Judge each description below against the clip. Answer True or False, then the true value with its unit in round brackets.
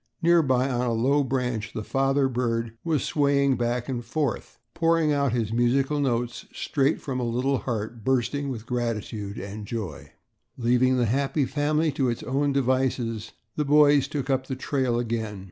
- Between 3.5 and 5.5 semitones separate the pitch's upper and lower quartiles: False (3.0 semitones)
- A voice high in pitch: False (130 Hz)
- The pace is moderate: True (165 wpm)